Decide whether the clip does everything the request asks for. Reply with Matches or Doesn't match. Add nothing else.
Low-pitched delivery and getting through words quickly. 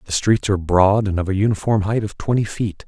Matches